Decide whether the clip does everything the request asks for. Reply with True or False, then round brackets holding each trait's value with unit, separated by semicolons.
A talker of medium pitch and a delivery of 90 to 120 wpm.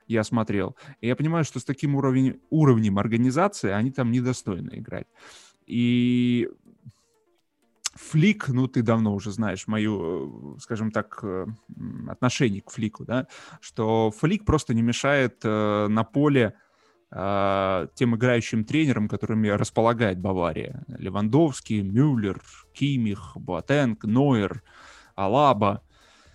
False (115 Hz; 115 wpm)